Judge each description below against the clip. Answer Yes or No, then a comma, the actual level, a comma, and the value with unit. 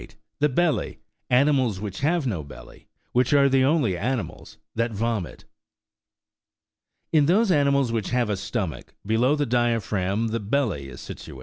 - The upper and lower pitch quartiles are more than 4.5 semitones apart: Yes, average, 5.1 semitones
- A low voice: Yes, low, 120 Hz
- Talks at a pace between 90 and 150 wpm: Yes, average, 145 wpm